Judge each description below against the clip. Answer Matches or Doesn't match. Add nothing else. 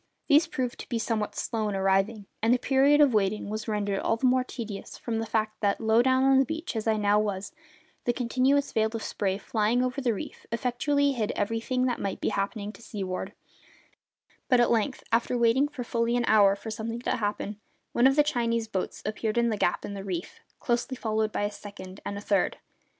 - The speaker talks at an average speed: Doesn't match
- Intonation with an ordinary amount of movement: Matches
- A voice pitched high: Matches